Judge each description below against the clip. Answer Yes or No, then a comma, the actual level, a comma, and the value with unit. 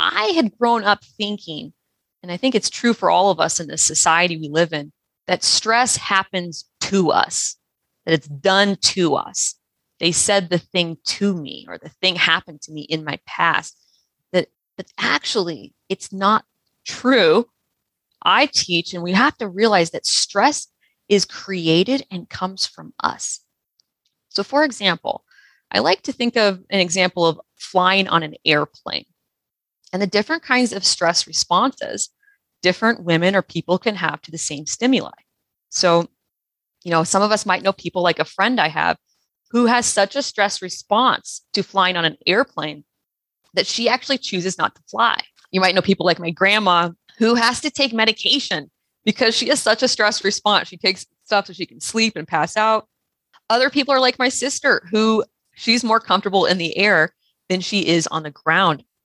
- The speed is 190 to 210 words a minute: No, average, 180 wpm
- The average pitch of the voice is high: Yes, high, 195 Hz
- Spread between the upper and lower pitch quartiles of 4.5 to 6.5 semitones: Yes, average, 4.9 semitones